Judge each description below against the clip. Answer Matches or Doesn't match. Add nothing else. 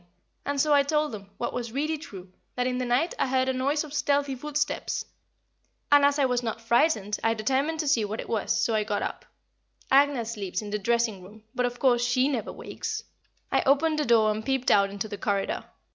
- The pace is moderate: Doesn't match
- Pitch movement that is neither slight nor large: Matches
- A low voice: Doesn't match